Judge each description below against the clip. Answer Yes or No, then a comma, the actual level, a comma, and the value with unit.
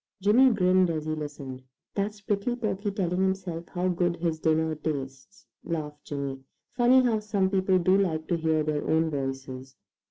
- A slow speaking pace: No, average, 165 wpm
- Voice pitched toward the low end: No, medium, 170 Hz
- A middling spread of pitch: Yes, average, 4.3 semitones